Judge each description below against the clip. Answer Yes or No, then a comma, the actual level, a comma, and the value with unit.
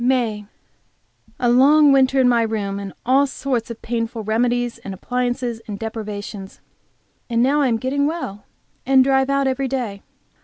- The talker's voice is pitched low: No, high, 245 Hz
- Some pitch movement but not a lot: Yes, average, 3.2 semitones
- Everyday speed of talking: Yes, average, 160 wpm